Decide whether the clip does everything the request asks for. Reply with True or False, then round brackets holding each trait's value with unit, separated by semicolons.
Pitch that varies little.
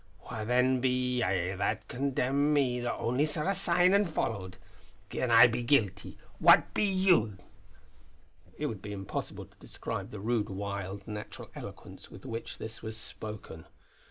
False (4.5 semitones)